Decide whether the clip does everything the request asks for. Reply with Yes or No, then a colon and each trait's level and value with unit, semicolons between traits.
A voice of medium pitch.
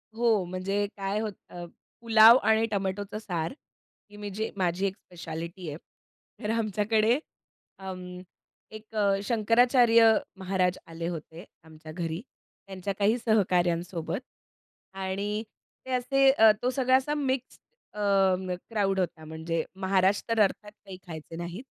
No: high, 195 Hz